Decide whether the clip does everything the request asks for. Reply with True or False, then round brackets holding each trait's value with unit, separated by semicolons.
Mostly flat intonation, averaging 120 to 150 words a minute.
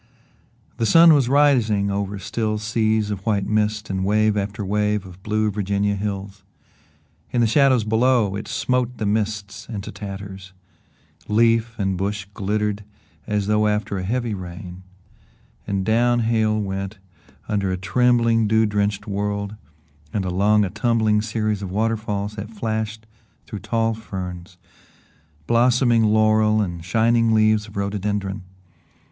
True (1.9 semitones; 140 wpm)